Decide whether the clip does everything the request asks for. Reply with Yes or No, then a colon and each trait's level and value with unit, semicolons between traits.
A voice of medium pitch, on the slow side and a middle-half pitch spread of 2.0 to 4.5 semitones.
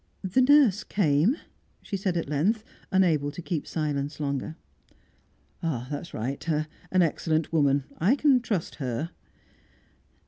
No: medium, 160 Hz; slow, 125 wpm; average, 5.0 semitones